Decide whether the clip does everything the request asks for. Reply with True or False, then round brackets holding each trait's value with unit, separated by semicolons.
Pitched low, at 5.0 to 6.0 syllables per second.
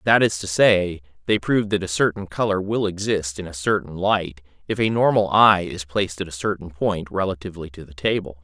True (95 Hz; 5.5 syllables/s)